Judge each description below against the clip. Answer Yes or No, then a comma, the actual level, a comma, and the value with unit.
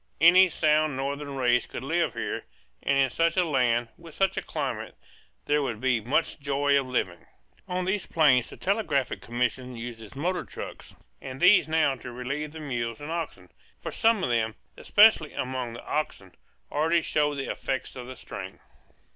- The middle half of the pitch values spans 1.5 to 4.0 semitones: No, average, 4.6 semitones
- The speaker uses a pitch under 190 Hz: Yes, medium, 140 Hz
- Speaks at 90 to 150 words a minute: No, average, 175 wpm